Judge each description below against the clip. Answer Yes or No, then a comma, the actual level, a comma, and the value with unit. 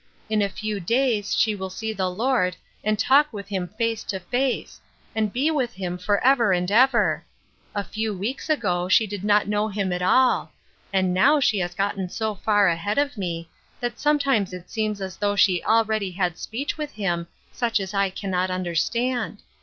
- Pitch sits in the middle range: No, high, 205 Hz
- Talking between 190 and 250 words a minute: Yes, average, 195 wpm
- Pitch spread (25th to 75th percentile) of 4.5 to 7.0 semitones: No, average, 3.7 semitones